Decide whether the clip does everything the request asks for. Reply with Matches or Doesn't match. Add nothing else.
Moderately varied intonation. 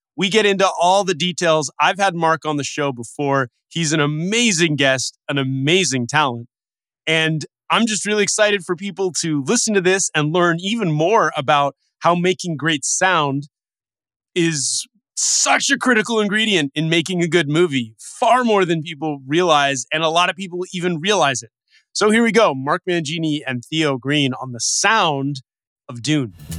Matches